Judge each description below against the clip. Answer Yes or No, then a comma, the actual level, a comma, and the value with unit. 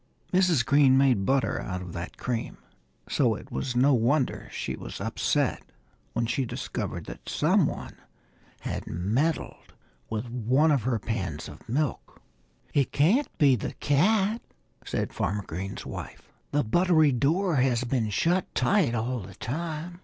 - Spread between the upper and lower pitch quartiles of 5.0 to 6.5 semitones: Yes, wide, 5.6 semitones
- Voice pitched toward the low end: Yes, low, 130 Hz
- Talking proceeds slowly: No, average, 150 wpm